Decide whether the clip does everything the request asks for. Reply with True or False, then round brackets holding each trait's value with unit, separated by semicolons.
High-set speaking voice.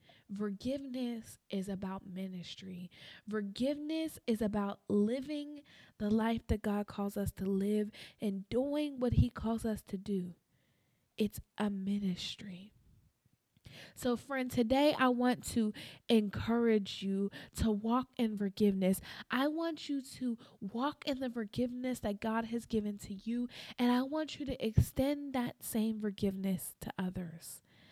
True (220 Hz)